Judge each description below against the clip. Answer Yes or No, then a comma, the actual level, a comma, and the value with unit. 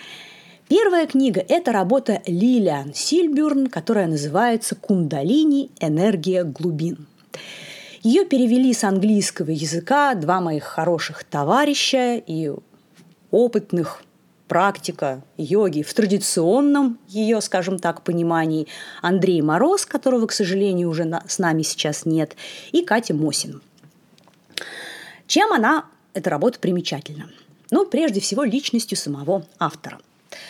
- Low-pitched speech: No, high, 190 Hz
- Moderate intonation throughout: No, wide, 6.5 semitones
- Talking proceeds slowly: Yes, slow, 105 wpm